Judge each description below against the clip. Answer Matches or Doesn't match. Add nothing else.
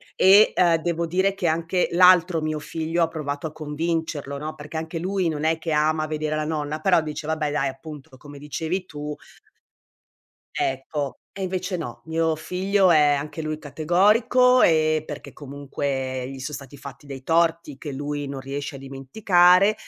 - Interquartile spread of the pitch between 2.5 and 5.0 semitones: Matches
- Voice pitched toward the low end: Doesn't match